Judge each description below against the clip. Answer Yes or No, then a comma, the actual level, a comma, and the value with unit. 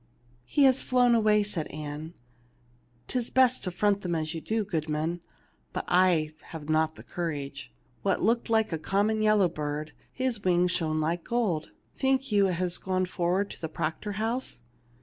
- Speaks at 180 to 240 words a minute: No, average, 170 wpm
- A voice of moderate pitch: Yes, medium, 180 Hz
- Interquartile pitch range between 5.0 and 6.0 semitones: Yes, wide, 5.4 semitones